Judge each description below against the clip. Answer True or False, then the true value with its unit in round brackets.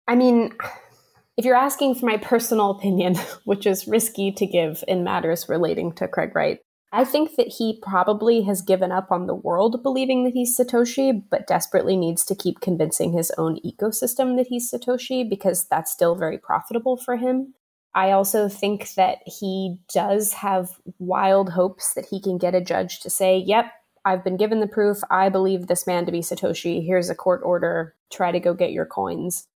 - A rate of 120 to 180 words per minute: False (190 wpm)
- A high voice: True (195 Hz)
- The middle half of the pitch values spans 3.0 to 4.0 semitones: False (4.5 semitones)